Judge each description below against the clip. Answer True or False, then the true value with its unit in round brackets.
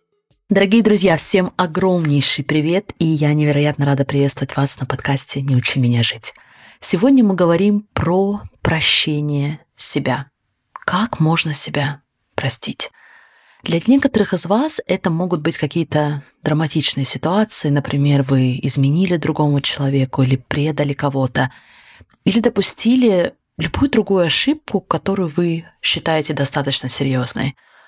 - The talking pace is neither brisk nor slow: True (120 wpm)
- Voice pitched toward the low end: False (155 Hz)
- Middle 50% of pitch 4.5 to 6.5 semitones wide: True (5.1 semitones)